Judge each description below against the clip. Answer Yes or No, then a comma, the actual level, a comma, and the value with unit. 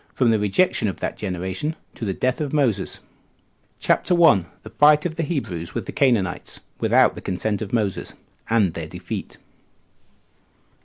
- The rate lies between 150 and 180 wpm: Yes, average, 155 wpm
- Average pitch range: No, wide, 7.6 semitones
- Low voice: Yes, low, 110 Hz